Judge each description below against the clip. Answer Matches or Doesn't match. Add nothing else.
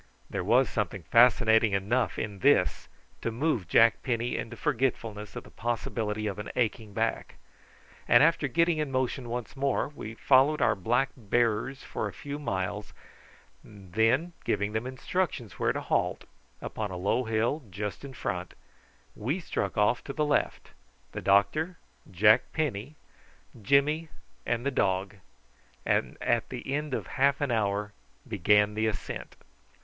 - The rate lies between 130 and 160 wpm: Matches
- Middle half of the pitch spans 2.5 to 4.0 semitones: Doesn't match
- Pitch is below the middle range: Matches